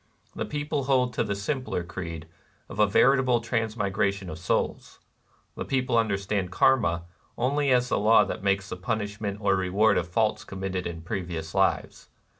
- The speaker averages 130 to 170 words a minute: Yes, average, 160 wpm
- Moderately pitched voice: No, low, 100 Hz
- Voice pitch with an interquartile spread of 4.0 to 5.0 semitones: Yes, average, 4.7 semitones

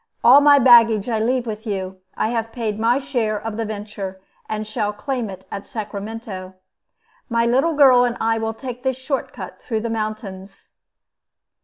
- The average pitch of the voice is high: Yes, high, 225 Hz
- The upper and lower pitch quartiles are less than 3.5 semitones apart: Yes, average, 2.8 semitones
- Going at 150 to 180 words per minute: Yes, average, 175 wpm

